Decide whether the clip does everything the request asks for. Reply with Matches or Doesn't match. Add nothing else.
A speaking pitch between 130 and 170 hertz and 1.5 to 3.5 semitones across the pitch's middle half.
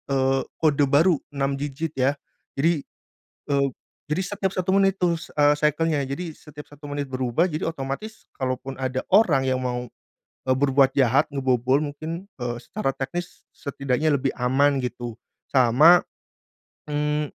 Matches